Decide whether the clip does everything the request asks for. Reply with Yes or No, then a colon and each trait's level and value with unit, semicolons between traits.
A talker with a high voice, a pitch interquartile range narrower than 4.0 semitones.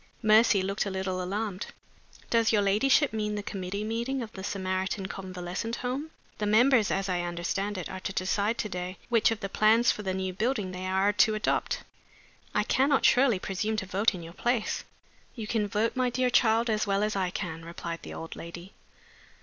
Yes: high, 205 Hz; average, 3.2 semitones